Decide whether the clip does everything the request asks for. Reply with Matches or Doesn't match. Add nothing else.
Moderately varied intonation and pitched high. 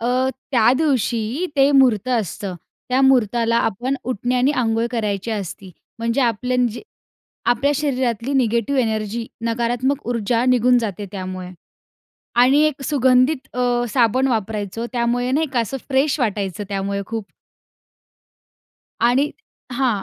Matches